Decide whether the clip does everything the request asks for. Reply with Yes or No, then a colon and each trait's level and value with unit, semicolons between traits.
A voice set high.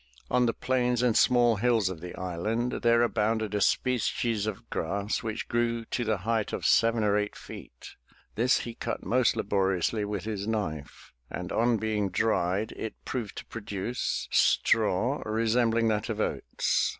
No: low, 110 Hz